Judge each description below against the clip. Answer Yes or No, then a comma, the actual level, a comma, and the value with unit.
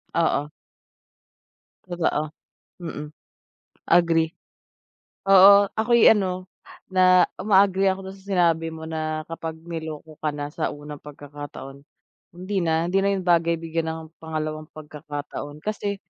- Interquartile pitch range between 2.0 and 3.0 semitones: No, average, 3.4 semitones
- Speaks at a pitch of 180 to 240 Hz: No, medium, 165 Hz